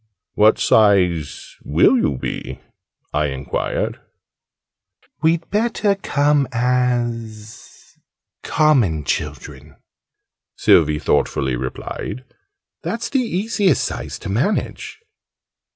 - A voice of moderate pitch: No, low, 120 Hz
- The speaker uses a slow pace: Yes, slow, 85 wpm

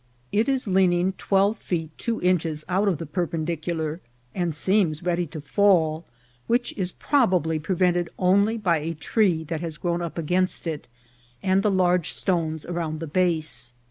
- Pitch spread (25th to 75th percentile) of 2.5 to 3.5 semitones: Yes, average, 2.9 semitones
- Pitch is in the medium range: Yes, medium, 175 Hz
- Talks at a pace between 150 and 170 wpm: Yes, average, 165 wpm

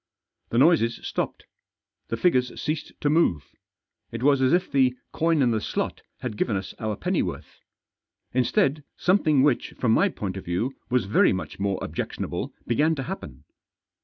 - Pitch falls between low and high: No, low, 130 Hz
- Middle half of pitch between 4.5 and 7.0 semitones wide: Yes, wide, 5.6 semitones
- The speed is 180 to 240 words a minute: No, average, 160 wpm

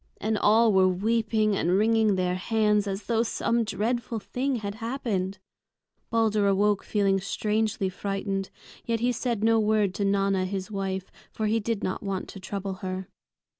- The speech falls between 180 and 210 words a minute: No, average, 165 wpm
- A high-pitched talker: Yes, high, 205 Hz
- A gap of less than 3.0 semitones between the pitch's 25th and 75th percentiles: Yes, narrow, 2.4 semitones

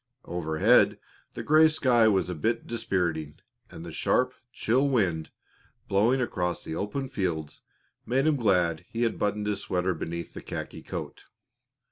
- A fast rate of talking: No, average, 150 wpm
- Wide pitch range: Yes, wide, 6.0 semitones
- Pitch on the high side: No, low, 100 Hz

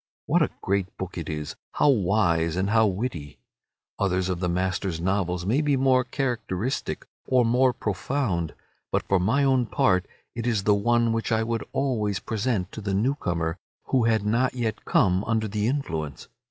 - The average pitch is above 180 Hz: No, low, 105 Hz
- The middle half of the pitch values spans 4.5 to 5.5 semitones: Yes, average, 4.8 semitones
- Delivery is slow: No, average, 180 wpm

